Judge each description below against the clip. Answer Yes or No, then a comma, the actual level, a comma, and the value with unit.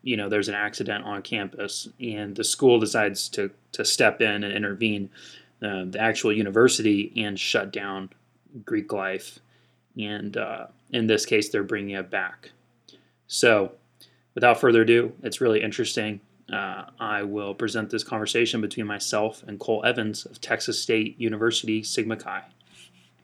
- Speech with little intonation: Yes, narrow, 1.7 semitones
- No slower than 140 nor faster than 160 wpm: Yes, average, 150 wpm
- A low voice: Yes, low, 105 Hz